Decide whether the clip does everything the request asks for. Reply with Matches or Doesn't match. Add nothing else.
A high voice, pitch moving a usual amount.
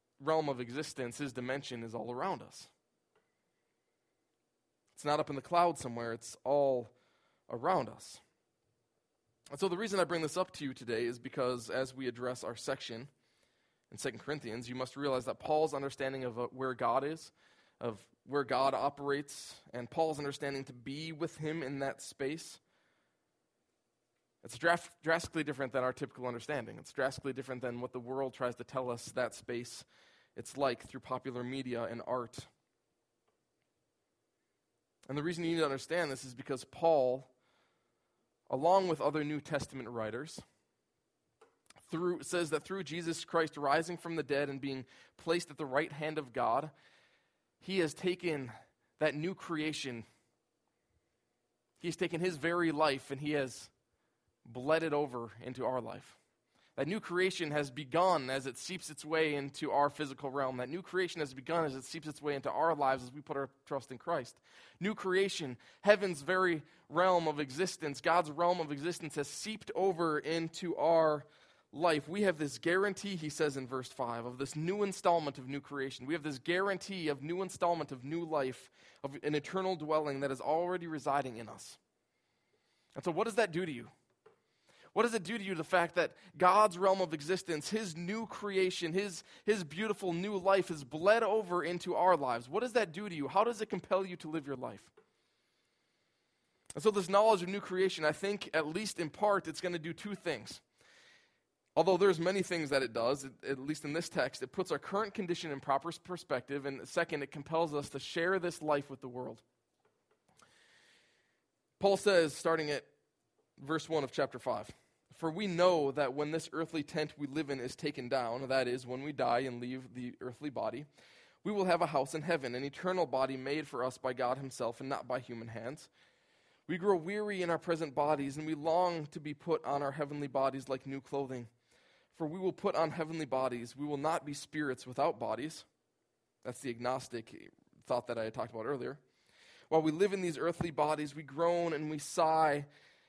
Doesn't match